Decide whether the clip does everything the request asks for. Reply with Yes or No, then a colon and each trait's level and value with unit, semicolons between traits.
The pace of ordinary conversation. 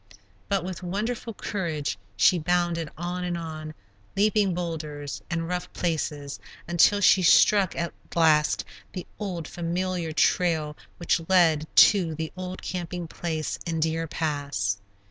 No: slow, 130 wpm